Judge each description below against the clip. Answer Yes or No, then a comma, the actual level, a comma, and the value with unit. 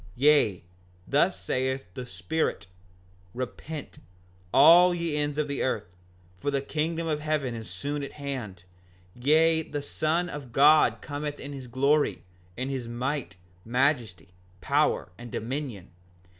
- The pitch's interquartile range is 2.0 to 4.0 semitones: Yes, average, 3.5 semitones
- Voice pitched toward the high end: No, medium, 140 Hz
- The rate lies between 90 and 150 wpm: Yes, average, 140 wpm